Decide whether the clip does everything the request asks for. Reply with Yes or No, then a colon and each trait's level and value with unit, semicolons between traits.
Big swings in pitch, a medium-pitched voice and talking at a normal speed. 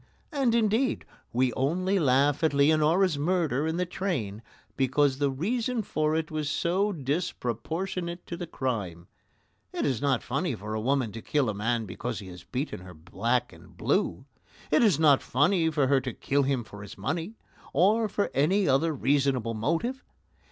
Yes: wide, 5.9 semitones; medium, 145 Hz; average, 175 wpm